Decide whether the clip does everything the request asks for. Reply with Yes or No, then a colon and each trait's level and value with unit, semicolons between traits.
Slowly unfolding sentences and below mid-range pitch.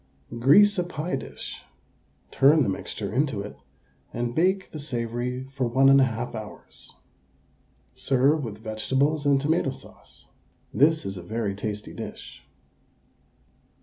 Yes: slow, 125 wpm; low, 130 Hz